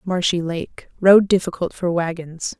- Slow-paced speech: Yes, slow, 115 wpm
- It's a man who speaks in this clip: No, female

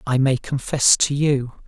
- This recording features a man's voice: Yes, male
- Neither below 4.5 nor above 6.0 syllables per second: No, 4.0 syllables/s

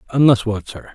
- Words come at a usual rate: Yes, average, 190 wpm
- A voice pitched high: No, low, 115 Hz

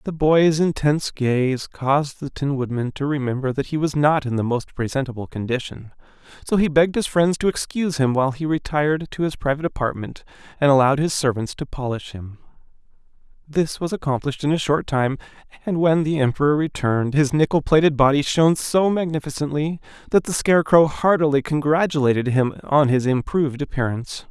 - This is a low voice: No, medium, 145 Hz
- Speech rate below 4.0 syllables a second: No, 5.7 syllables/s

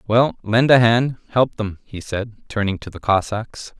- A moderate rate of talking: Yes, average, 190 wpm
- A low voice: Yes, low, 110 Hz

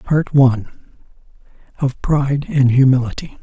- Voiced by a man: Yes, male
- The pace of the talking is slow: Yes, slow, 105 wpm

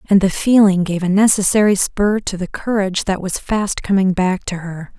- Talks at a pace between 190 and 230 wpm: Yes, fast, 205 wpm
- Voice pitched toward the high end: Yes, high, 195 Hz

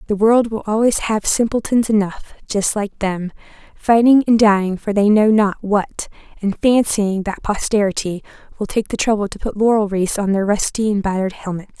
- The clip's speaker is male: No, female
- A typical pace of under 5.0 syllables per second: No, 5.1 syllables/s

